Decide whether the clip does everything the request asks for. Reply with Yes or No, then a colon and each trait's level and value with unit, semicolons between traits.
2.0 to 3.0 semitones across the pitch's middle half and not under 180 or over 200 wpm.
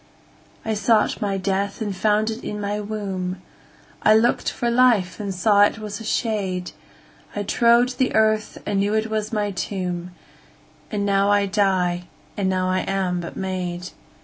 No: narrow, 2.5 semitones; average, 155 wpm